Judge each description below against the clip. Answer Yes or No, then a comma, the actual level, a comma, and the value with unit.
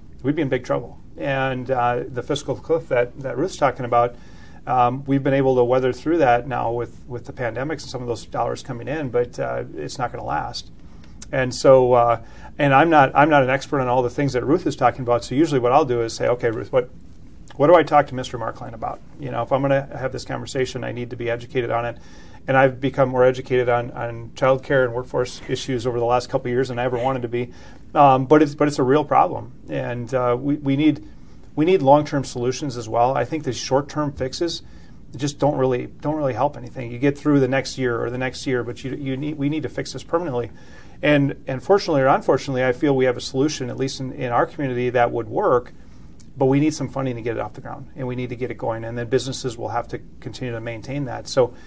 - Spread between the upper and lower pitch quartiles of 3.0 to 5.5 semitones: No, narrow, 2.4 semitones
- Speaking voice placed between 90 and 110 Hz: No, low, 130 Hz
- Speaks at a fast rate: Yes, fast, 255 wpm